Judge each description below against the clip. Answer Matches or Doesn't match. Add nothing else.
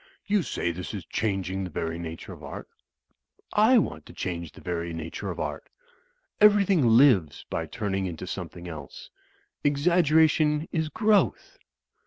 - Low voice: Matches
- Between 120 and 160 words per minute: Matches